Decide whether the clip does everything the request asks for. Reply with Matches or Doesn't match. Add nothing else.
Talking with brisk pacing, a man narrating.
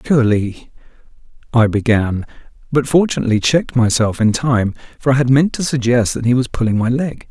Doesn't match